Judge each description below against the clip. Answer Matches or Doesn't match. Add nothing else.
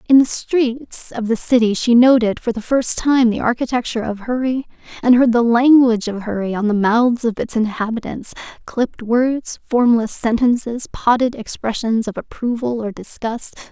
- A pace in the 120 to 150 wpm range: Doesn't match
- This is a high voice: Matches